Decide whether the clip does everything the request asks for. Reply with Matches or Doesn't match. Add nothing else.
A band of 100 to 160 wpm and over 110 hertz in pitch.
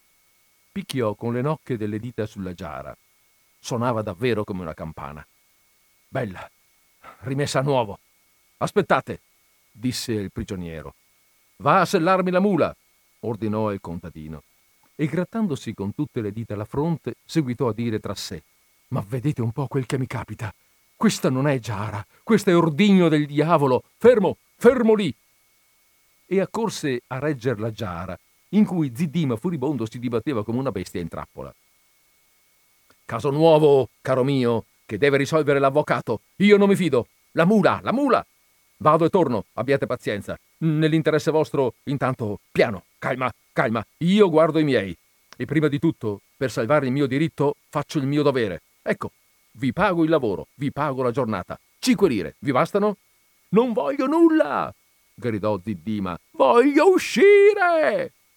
Matches